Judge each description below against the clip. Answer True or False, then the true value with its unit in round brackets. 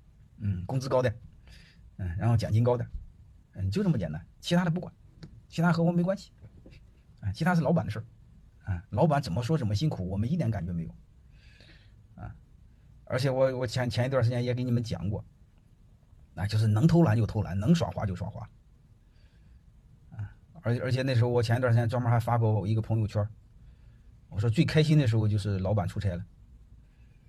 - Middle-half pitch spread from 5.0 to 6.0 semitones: False (4.0 semitones)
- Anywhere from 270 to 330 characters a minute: True (285 characters per minute)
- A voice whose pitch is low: True (110 Hz)